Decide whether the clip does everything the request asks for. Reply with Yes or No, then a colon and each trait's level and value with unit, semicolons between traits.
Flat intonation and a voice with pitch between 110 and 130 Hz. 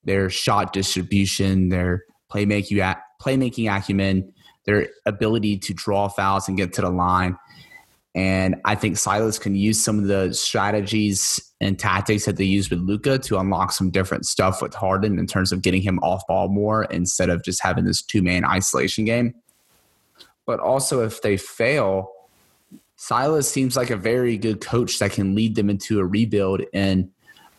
No: narrow, 2.3 semitones; low, 100 Hz